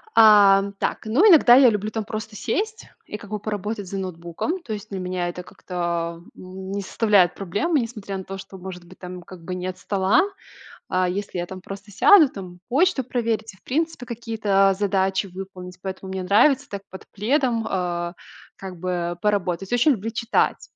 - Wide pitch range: No, average, 3.5 semitones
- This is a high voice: Yes, high, 195 Hz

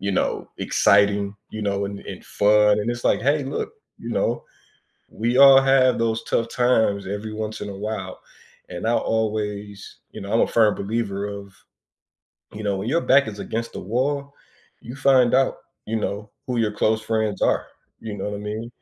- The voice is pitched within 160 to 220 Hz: No, low, 110 Hz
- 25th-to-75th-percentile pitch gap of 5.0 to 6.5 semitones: No, average, 2.8 semitones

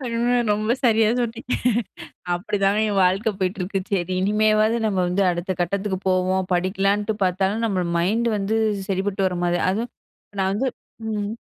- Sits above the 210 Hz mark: No, high, 200 Hz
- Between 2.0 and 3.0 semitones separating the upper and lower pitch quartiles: Yes, narrow, 2.5 semitones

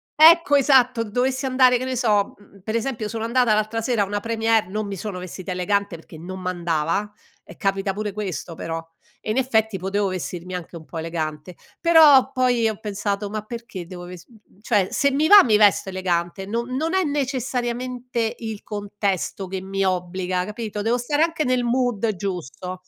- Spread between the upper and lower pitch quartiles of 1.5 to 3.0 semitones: No, average, 4.9 semitones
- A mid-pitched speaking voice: No, high, 210 Hz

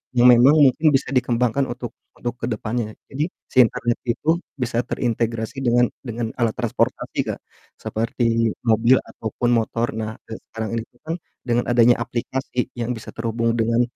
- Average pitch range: No, narrow, 1.3 semitones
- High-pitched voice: No, low, 120 Hz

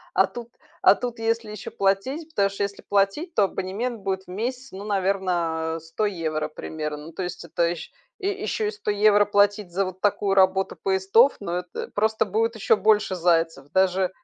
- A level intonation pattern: No, average, 3.2 semitones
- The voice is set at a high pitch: Yes, high, 195 Hz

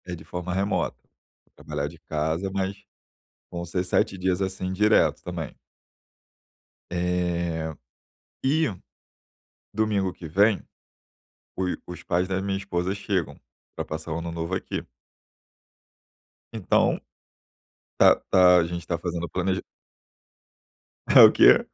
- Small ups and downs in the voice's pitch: Yes, narrow, 2.1 semitones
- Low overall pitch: Yes, very low, 90 Hz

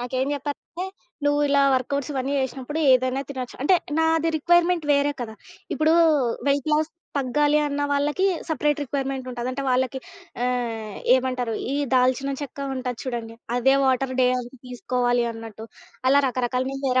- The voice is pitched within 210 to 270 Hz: Yes, very high, 265 Hz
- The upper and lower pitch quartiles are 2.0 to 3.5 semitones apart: Yes, narrow, 2.5 semitones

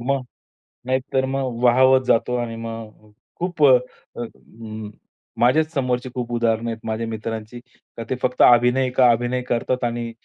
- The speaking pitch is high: No, low, 120 Hz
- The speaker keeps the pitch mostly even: Yes, narrow, 2.1 semitones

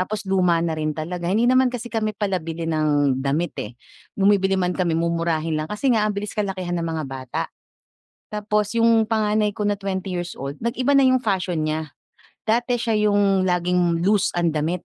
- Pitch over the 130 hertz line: Yes, medium, 185 Hz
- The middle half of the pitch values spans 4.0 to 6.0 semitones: Yes, average, 4.3 semitones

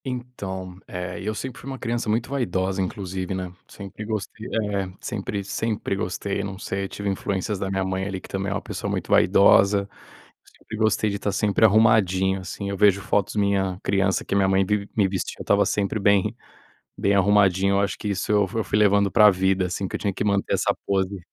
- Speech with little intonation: Yes, narrow, 1.6 semitones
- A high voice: No, low, 100 Hz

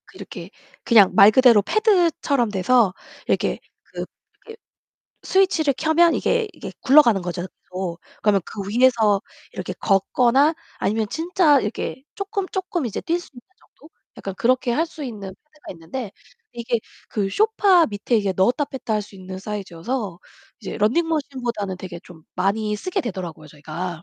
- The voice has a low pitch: No, high, 235 Hz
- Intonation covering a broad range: Yes, wide, 7.8 semitones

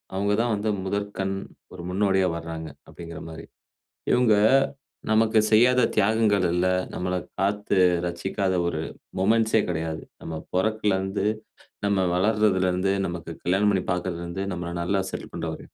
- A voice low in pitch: Yes, very low, 95 Hz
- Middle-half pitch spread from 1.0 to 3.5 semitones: Yes, average, 3.0 semitones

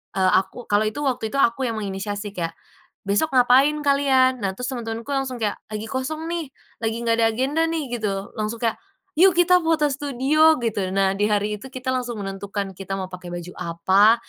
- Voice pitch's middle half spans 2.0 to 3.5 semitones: No, average, 5.0 semitones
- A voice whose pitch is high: Yes, high, 230 Hz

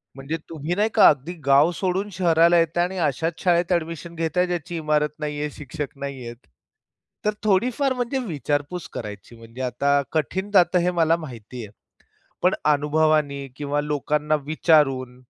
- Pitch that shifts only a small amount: No, average, 3.6 semitones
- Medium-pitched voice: Yes, medium, 155 Hz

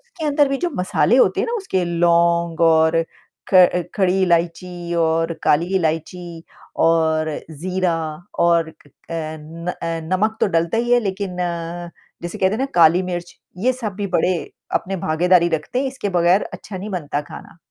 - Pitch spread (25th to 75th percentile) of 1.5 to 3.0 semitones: Yes, average, 2.7 semitones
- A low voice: No, medium, 175 Hz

